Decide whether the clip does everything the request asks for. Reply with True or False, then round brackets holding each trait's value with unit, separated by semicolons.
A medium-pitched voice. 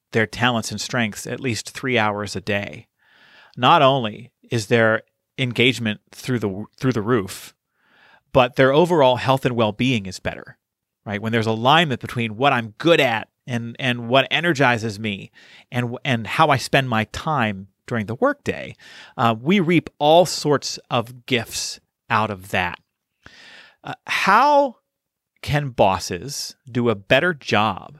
False (120 Hz)